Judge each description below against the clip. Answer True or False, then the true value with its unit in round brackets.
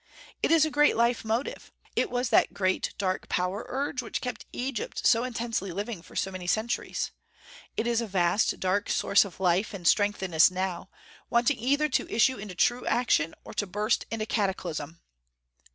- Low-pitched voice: False (210 Hz)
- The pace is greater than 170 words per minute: True (185 wpm)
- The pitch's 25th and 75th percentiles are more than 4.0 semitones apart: True (4.5 semitones)